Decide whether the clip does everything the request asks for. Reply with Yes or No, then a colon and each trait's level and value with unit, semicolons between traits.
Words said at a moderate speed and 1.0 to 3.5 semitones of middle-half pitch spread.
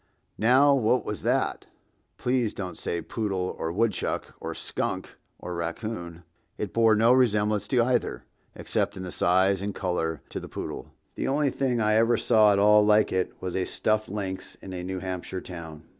No: average, 175 wpm; average, 3.9 semitones